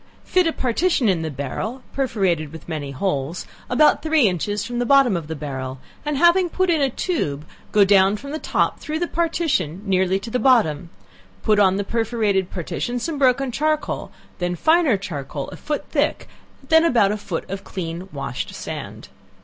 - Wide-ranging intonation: Yes, wide, 8.5 semitones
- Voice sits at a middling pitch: No, high, 210 Hz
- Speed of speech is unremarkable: Yes, average, 185 wpm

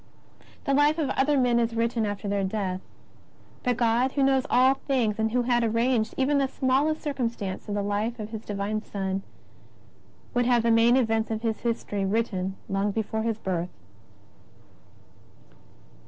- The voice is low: No, high, 230 Hz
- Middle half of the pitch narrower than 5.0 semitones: Yes, average, 3.5 semitones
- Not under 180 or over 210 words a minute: No, average, 165 wpm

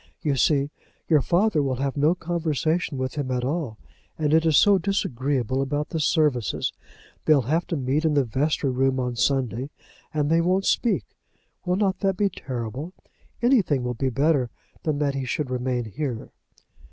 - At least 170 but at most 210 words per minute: Yes, average, 175 wpm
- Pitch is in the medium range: Yes, medium, 145 Hz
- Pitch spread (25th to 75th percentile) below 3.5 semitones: No, average, 4.0 semitones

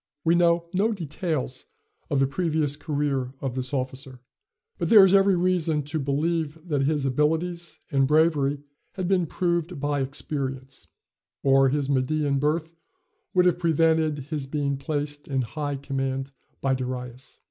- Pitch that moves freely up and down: No, average, 3.5 semitones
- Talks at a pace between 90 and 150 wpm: Yes, average, 145 wpm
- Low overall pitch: No, medium, 145 Hz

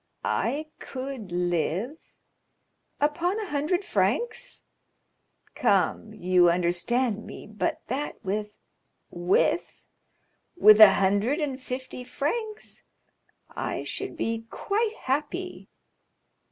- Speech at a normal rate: No, slow, 90 wpm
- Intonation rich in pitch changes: Yes, wide, 7.0 semitones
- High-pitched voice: Yes, very high, 255 Hz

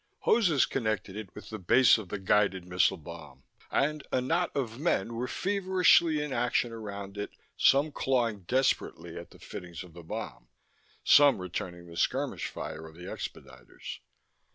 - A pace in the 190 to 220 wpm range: No, average, 160 wpm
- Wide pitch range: Yes, wide, 7.3 semitones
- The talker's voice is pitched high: No, low, 110 Hz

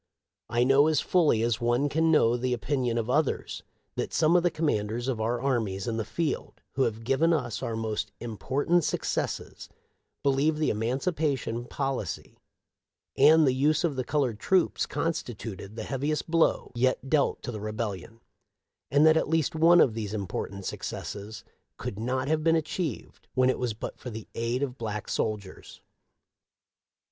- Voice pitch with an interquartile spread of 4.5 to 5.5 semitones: Yes, average, 5.2 semitones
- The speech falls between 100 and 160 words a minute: No, average, 175 wpm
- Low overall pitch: Yes, low, 130 Hz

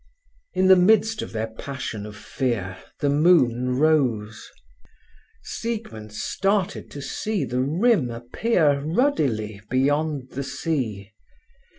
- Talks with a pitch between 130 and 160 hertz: Yes, medium, 140 Hz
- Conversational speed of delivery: No, slow, 110 wpm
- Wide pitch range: Yes, wide, 7.9 semitones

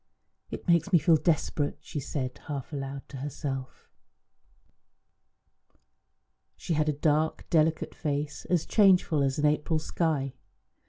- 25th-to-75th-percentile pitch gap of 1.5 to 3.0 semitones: Yes, narrow, 2.4 semitones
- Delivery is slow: Yes, slow, 125 wpm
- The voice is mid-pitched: Yes, medium, 150 Hz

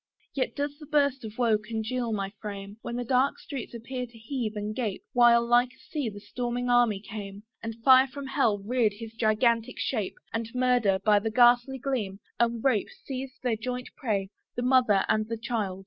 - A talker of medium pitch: No, high, 235 Hz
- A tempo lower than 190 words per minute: No, average, 195 wpm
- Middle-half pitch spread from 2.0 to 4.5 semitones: Yes, average, 2.9 semitones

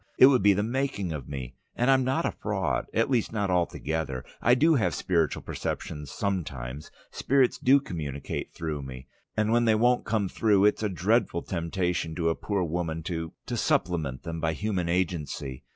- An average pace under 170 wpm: No, average, 185 wpm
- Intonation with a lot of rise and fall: Yes, wide, 5.7 semitones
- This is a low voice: Yes, very low, 90 Hz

